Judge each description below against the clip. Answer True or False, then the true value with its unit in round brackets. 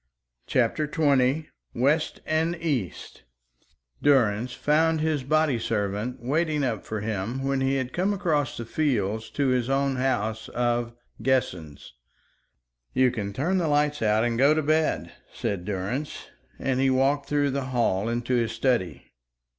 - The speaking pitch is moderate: False (130 Hz)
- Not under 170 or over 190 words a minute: False (145 wpm)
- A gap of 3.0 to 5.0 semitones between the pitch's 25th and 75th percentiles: True (4.3 semitones)